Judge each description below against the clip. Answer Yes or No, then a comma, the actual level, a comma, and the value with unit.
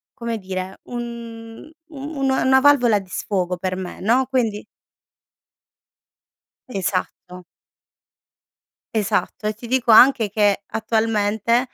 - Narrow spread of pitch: No, average, 3.7 semitones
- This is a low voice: No, high, 225 Hz